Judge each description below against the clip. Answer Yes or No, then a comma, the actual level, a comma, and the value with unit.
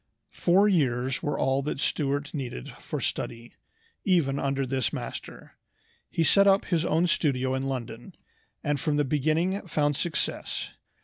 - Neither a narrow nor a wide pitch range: Yes, average, 3.9 semitones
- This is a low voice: No, medium, 145 Hz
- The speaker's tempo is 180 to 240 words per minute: No, average, 145 wpm